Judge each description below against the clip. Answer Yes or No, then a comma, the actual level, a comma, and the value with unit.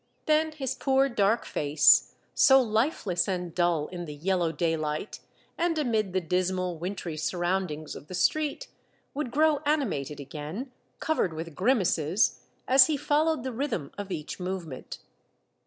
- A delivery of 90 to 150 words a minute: Yes, average, 145 wpm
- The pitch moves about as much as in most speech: No, wide, 8.3 semitones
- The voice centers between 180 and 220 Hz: Yes, high, 190 Hz